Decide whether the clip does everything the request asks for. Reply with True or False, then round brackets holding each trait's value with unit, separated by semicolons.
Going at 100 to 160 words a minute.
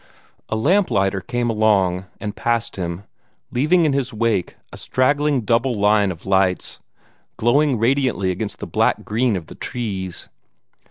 True (150 wpm)